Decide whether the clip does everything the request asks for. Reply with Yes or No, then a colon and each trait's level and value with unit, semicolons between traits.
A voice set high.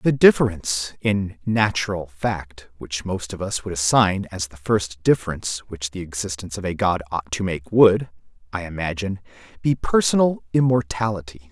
No: very low, 95 Hz